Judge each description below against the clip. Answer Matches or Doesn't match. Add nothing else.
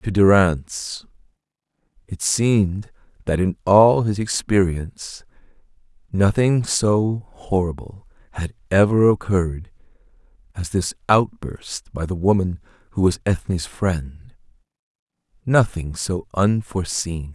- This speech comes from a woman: Doesn't match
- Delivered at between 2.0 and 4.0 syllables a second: Matches